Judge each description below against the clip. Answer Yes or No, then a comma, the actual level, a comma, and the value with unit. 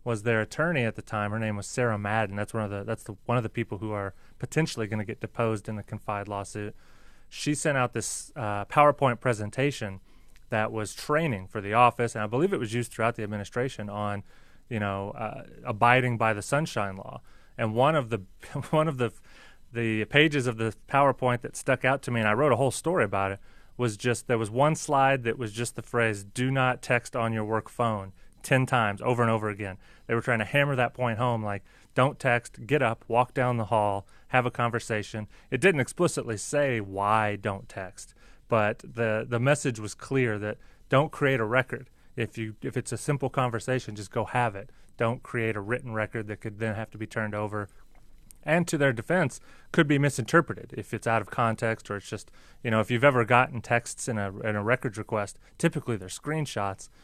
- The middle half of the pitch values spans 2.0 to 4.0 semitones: Yes, average, 3.3 semitones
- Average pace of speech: No, fast, 215 wpm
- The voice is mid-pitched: No, low, 115 Hz